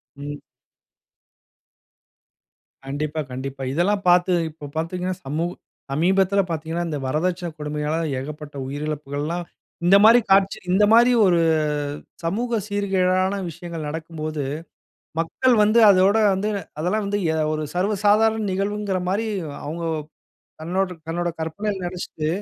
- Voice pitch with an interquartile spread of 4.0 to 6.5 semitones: Yes, average, 4.4 semitones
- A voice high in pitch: No, medium, 175 Hz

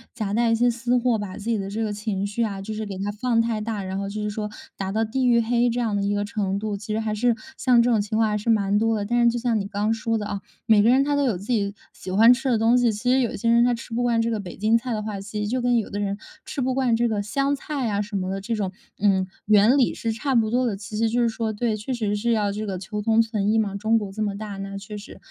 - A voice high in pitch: Yes, high, 220 Hz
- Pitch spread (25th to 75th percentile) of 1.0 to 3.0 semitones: Yes, narrow, 2.5 semitones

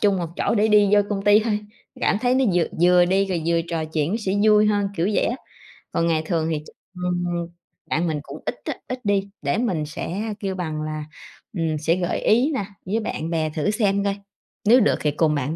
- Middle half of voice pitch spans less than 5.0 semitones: Yes, average, 4.4 semitones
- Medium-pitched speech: Yes, medium, 180 Hz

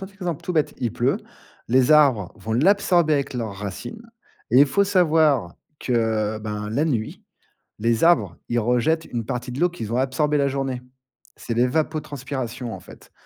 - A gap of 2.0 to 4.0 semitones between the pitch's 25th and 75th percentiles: No, average, 5.2 semitones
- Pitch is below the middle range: Yes, low, 130 Hz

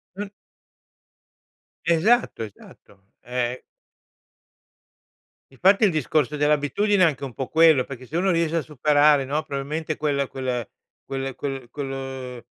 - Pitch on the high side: No, medium, 145 Hz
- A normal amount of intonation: Yes, average, 3.3 semitones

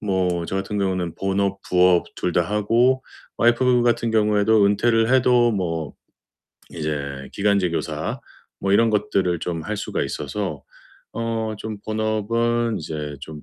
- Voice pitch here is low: Yes, low, 100 Hz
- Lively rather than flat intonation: No, average, 4.3 semitones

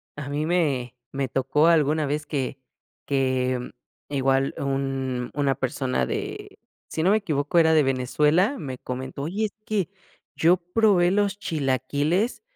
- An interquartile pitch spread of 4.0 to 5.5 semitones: Yes, average, 4.3 semitones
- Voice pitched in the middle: Yes, medium, 145 Hz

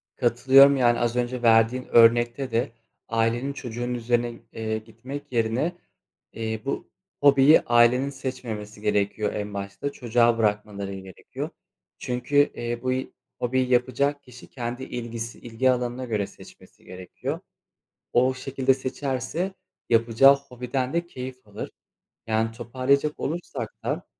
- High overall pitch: No, low, 120 Hz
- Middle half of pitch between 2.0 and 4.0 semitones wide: Yes, narrow, 2.5 semitones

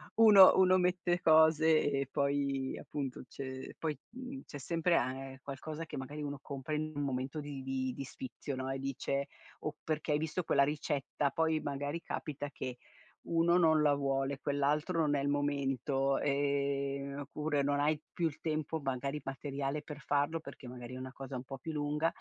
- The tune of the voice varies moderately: No, narrow, 2.3 semitones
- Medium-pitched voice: Yes, medium, 145 Hz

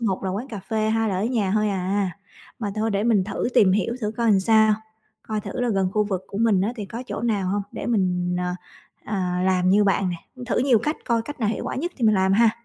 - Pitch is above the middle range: Yes, high, 210 Hz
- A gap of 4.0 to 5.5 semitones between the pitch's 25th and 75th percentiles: No, average, 3.0 semitones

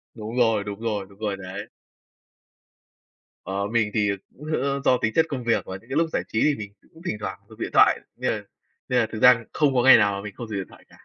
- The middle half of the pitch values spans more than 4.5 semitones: No, average, 3.8 semitones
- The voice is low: Yes, low, 110 Hz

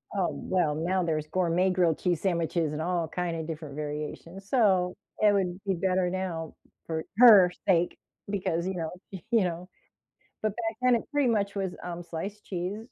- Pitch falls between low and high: Yes, medium, 180 Hz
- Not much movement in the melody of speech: No, average, 3.0 semitones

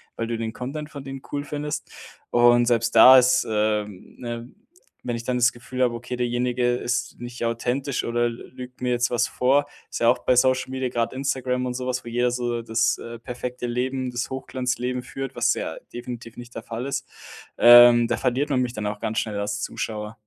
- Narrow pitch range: Yes, narrow, 1.4 semitones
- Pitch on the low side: Yes, low, 120 Hz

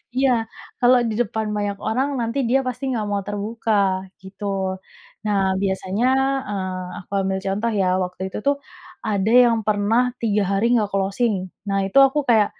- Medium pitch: No, high, 210 Hz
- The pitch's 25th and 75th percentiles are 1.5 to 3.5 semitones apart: Yes, average, 2.9 semitones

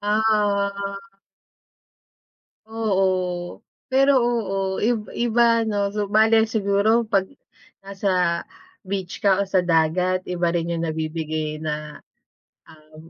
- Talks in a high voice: Yes, high, 195 Hz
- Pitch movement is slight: No, average, 4.0 semitones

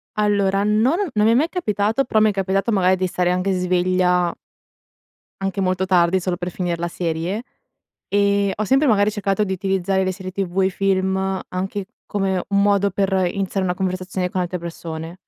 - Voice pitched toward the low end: No, high, 190 Hz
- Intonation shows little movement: Yes, narrow, 1.8 semitones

